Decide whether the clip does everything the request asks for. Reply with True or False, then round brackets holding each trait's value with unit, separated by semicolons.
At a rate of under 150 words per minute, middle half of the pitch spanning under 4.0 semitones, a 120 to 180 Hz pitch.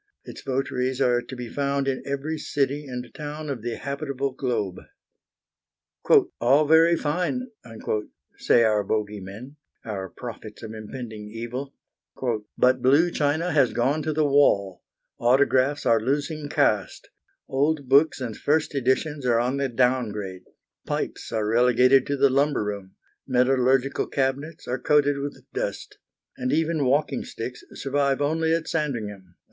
True (140 wpm; 3.4 semitones; 135 Hz)